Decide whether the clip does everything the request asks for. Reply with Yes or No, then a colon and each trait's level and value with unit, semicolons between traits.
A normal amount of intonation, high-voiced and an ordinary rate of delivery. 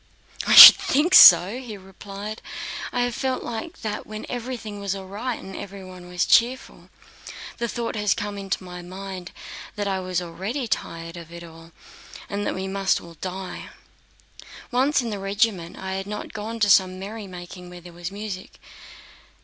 Yes: average, 3.2 semitones; high, 195 Hz; average, 175 wpm